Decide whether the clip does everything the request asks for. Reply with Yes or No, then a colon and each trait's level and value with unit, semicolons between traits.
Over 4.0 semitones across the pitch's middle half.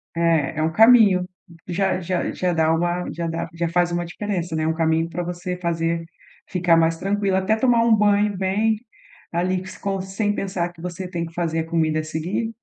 No: average, 2.7 semitones